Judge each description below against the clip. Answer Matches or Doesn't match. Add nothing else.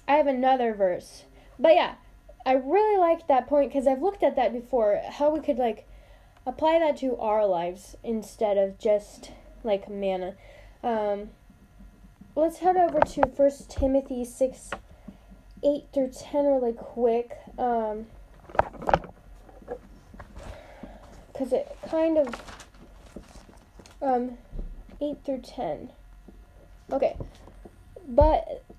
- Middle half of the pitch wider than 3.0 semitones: Matches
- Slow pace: Matches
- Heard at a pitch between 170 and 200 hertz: Doesn't match